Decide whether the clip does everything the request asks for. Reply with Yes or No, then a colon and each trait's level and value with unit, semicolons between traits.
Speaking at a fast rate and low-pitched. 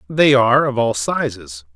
No: average, 170 wpm; low, 115 Hz